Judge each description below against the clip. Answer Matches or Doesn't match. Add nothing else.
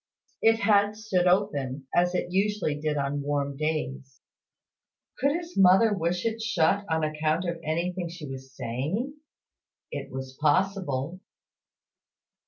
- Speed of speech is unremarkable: Doesn't match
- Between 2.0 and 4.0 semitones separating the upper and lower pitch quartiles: Doesn't match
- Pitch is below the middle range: Doesn't match